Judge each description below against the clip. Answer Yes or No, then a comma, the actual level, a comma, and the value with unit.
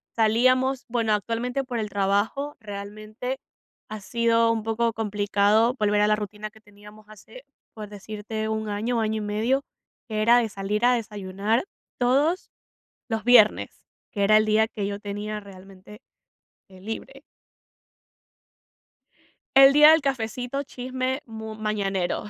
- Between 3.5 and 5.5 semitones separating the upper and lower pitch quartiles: No, average, 2.7 semitones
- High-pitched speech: Yes, high, 220 Hz